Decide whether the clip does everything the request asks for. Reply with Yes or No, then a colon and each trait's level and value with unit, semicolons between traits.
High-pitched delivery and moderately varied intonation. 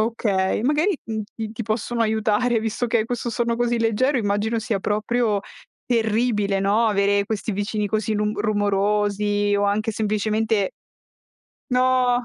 No: high, 215 Hz; narrow, 2.3 semitones